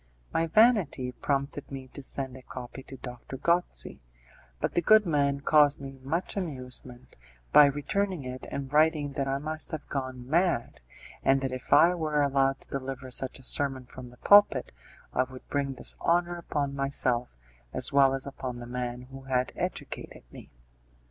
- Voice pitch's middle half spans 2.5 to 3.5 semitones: Yes, average, 2.8 semitones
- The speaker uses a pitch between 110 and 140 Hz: Yes, low, 135 Hz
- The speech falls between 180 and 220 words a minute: No, average, 170 wpm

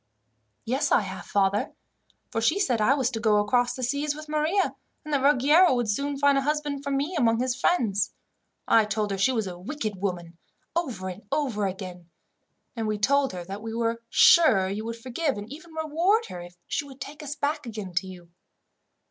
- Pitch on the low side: No, high, 245 Hz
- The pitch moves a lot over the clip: Yes, wide, 5.8 semitones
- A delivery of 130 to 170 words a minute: No, fast, 205 wpm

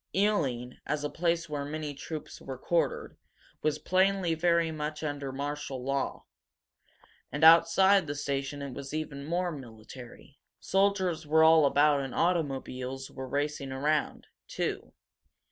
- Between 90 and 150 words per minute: Yes, slow, 135 wpm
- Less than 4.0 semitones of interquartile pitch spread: Yes, average, 3.2 semitones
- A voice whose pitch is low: No, medium, 150 Hz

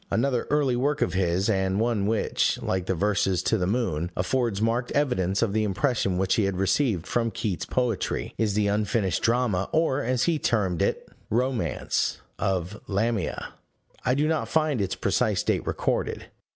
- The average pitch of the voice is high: No, low, 110 Hz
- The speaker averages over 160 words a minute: Yes, average, 170 wpm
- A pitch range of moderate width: Yes, average, 4.6 semitones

